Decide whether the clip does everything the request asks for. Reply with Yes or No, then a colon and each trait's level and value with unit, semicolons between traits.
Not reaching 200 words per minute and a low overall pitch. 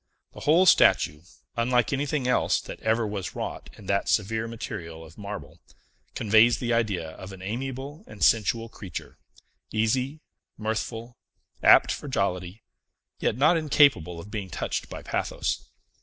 Yes: average, 140 wpm; low, 110 Hz